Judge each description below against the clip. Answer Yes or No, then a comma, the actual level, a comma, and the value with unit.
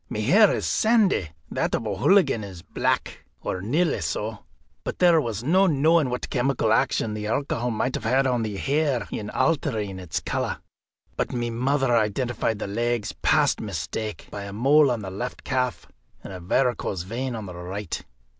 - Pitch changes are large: No, average, 4.7 semitones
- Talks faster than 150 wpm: Yes, average, 175 wpm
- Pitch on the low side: Yes, low, 120 Hz